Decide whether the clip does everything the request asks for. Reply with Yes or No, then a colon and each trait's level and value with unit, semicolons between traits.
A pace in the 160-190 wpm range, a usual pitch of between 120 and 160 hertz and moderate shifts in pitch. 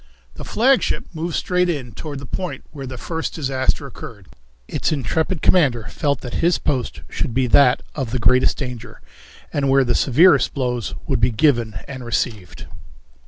Yes: average, 165 wpm; low, 135 Hz; average, 4.1 semitones